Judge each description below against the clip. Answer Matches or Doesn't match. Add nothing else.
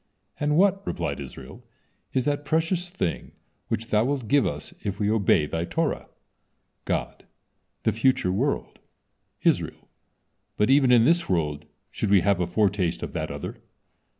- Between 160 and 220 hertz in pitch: Doesn't match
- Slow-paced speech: Doesn't match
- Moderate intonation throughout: Doesn't match